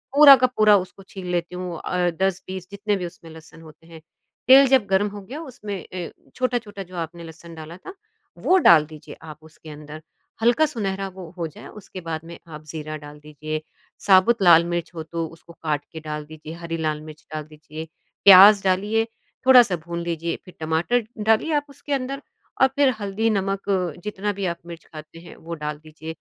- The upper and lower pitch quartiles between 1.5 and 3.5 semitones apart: No, average, 4.5 semitones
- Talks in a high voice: No, medium, 175 Hz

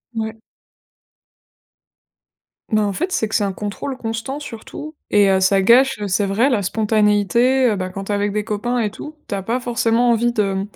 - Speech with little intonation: No, average, 3.0 semitones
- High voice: Yes, high, 220 Hz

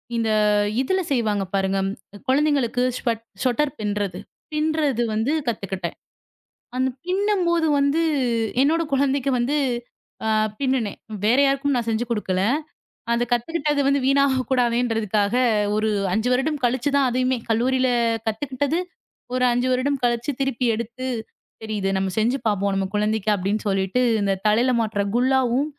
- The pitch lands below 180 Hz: No, high, 245 Hz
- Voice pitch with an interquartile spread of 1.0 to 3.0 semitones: No, average, 4.2 semitones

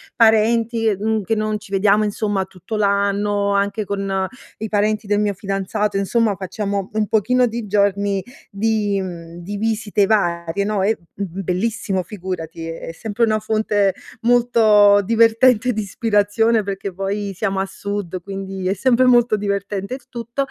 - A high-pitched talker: Yes, high, 205 Hz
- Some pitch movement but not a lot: No, narrow, 2.0 semitones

